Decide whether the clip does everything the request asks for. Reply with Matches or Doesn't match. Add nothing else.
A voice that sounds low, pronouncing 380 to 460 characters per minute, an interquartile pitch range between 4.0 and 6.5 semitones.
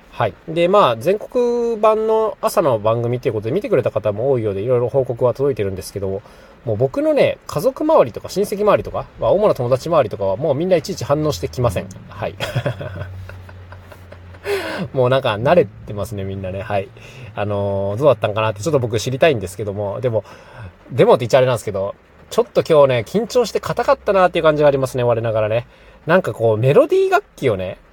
Doesn't match